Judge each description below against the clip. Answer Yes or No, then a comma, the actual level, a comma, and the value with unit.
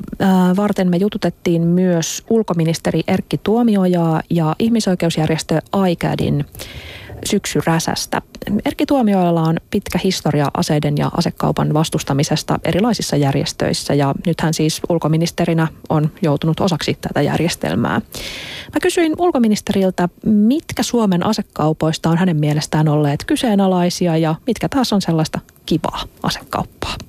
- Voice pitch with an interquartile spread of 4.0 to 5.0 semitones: Yes, average, 4.6 semitones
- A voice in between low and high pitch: Yes, medium, 175 Hz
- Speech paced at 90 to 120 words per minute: Yes, average, 110 wpm